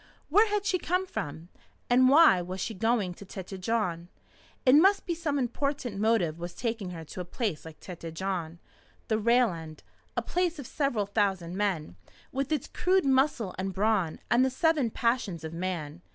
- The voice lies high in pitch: Yes, high, 215 Hz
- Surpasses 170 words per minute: Yes, average, 180 wpm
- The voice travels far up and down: Yes, wide, 7.2 semitones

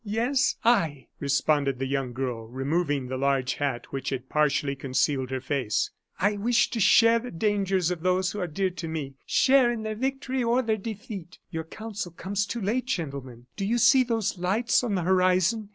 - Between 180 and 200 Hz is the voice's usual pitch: Yes, medium, 185 Hz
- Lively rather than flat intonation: Yes, wide, 8.2 semitones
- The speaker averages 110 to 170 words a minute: No, average, 190 wpm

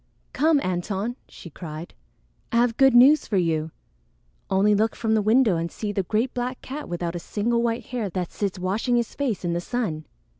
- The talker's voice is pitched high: Yes, high, 215 Hz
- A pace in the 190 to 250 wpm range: Yes, average, 195 wpm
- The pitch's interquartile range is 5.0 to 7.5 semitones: Yes, average, 5.3 semitones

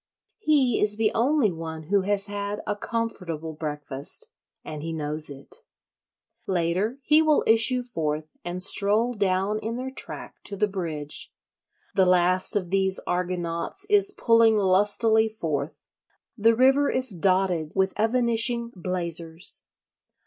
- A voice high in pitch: Yes, high, 200 Hz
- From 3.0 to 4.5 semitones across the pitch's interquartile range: No, average, 5.2 semitones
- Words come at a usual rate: No, slow, 130 wpm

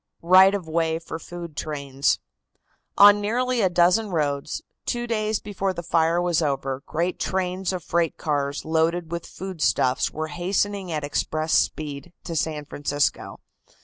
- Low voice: No, medium, 170 Hz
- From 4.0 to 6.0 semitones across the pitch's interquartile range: No, average, 3.6 semitones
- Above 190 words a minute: No, average, 145 wpm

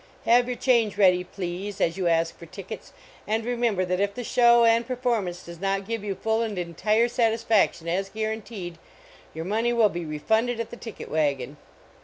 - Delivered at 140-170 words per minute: No, average, 185 wpm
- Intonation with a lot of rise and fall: No, average, 4.5 semitones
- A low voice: No, high, 205 Hz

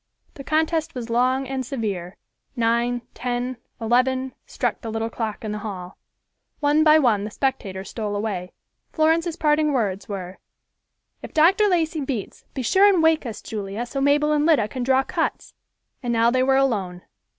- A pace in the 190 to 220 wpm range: No, average, 170 wpm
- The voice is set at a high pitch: Yes, very high, 250 Hz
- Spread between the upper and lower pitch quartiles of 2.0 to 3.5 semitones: No, wide, 5.4 semitones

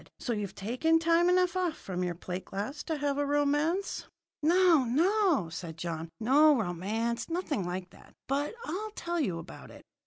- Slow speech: No, average, 175 wpm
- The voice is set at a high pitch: Yes, very high, 285 Hz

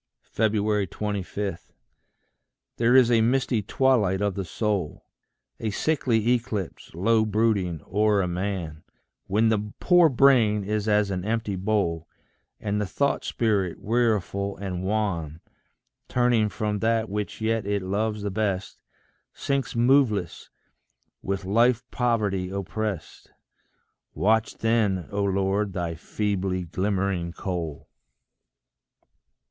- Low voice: Yes, low, 105 Hz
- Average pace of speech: No, slow, 115 wpm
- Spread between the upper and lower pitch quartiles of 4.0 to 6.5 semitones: No, average, 2.8 semitones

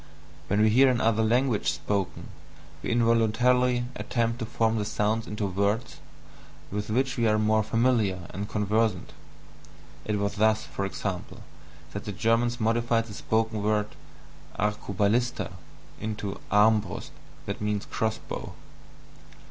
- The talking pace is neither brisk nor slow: No, slow, 125 wpm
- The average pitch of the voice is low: Yes, low, 110 Hz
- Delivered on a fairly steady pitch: Yes, narrow, 2.0 semitones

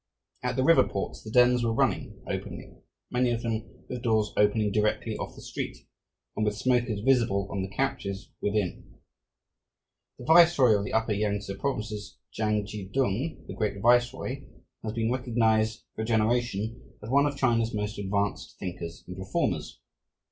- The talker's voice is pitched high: No, low, 110 Hz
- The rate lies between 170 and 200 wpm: No, average, 160 wpm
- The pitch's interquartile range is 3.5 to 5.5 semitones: No, average, 3.1 semitones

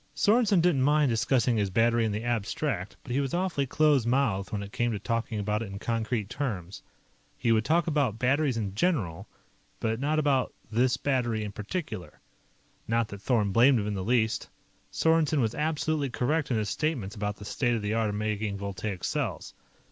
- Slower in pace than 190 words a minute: No, average, 195 wpm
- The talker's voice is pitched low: Yes, low, 115 Hz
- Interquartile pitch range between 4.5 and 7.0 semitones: Yes, average, 5.2 semitones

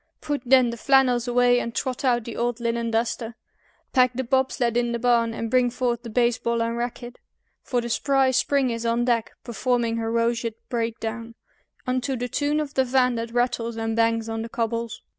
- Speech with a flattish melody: Yes, narrow, 1.5 semitones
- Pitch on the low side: No, high, 240 Hz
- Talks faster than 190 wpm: Yes, average, 200 wpm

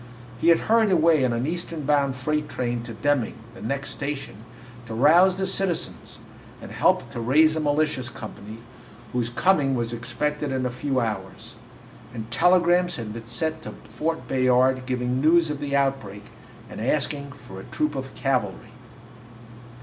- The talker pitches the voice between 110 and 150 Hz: Yes, low, 135 Hz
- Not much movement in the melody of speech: No, average, 4.5 semitones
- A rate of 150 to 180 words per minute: Yes, average, 165 wpm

